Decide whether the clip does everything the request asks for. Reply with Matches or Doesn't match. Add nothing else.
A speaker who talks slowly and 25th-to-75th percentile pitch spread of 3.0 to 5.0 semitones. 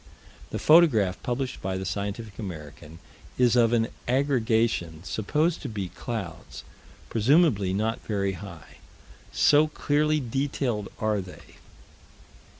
Doesn't match